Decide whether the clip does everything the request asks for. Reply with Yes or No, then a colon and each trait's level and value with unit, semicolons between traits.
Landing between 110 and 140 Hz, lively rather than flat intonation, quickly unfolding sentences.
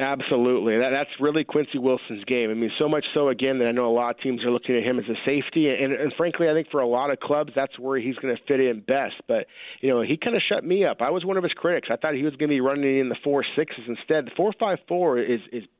No: low, 135 Hz; average, 3.5 semitones; fast, 305 wpm